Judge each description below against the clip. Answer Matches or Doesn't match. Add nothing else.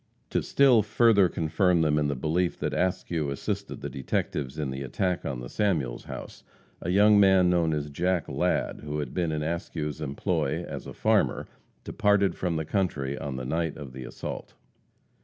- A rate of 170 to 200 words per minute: Matches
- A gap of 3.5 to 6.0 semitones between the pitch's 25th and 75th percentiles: Matches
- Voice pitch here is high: Doesn't match